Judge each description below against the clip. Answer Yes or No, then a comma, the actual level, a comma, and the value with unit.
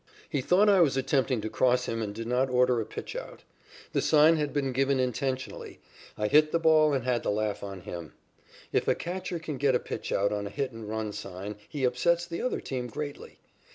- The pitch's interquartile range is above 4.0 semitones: Yes, average, 5.3 semitones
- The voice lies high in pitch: No, low, 130 Hz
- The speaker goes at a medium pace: No, fast, 215 wpm